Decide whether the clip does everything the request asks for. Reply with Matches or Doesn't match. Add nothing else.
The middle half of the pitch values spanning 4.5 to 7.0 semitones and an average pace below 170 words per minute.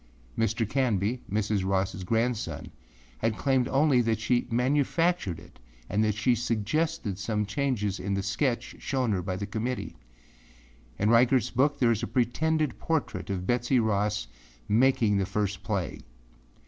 Doesn't match